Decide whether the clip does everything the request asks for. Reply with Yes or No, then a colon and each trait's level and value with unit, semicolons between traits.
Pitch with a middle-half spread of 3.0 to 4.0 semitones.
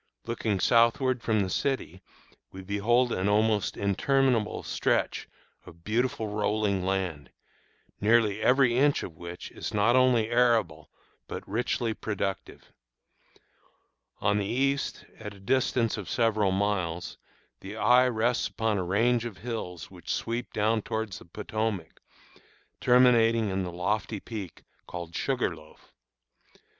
Yes: average, 3.5 semitones